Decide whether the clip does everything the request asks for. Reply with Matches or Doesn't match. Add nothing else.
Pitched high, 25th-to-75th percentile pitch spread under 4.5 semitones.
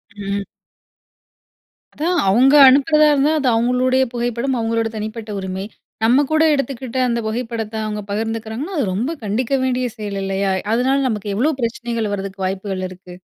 Matches